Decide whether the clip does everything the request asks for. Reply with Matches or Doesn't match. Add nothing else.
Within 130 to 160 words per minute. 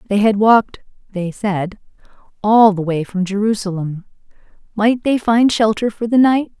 Matches